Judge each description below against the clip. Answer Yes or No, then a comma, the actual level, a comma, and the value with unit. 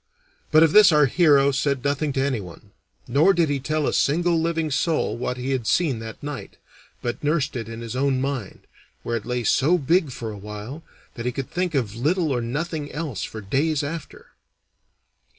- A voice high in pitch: No, medium, 140 Hz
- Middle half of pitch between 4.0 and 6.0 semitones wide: Yes, average, 4.5 semitones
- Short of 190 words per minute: No, average, 195 wpm